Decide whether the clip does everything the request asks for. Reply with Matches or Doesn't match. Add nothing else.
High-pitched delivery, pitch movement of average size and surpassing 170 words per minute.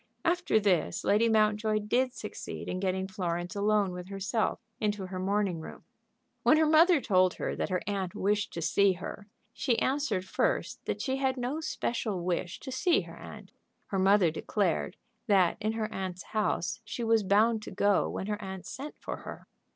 Matches